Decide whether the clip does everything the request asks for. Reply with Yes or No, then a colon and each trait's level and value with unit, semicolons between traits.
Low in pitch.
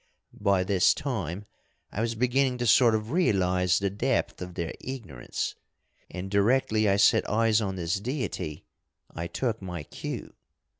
Yes: low, 100 Hz